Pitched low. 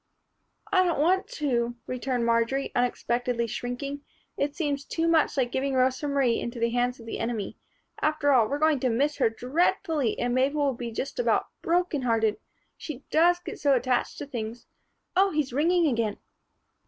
No: very high, 265 Hz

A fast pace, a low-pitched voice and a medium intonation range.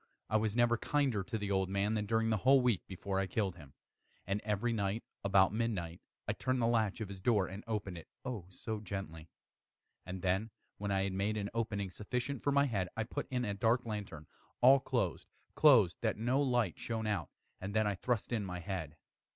Yes: fast, 210 wpm; low, 105 Hz; average, 3.3 semitones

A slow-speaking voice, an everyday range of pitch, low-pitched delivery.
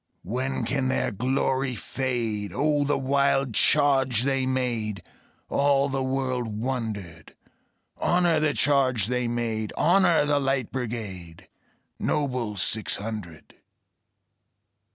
Yes: slow, 110 wpm; average, 3.7 semitones; low, 130 Hz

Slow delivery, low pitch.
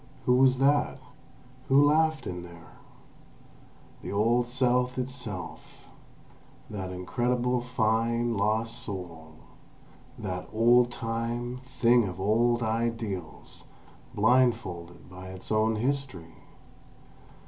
Yes: slow, 95 wpm; low, 115 Hz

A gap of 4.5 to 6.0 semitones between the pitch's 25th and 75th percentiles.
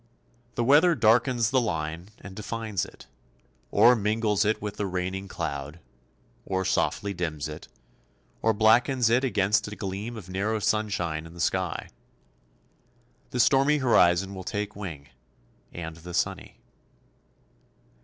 No: average, 4.1 semitones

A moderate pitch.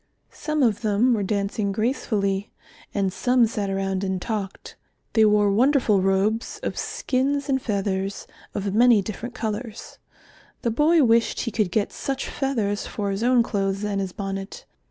No: high, 215 Hz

